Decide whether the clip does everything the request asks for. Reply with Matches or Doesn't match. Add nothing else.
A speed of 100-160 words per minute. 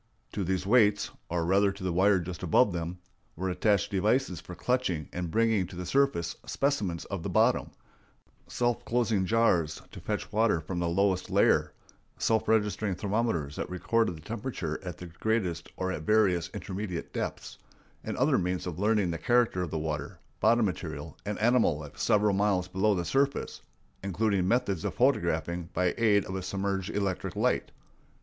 Doesn't match